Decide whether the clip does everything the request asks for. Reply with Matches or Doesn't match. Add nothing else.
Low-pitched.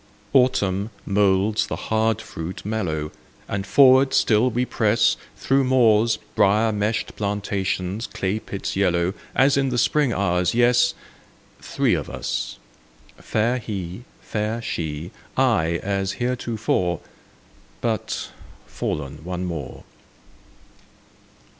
Matches